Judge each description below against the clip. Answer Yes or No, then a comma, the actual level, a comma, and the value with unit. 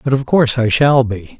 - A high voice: No, low, 125 Hz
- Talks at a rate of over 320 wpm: No, fast, 260 wpm